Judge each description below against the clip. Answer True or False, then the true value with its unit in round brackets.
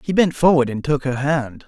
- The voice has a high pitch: False (140 Hz)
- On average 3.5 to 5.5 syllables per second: True (5.1 syllables/s)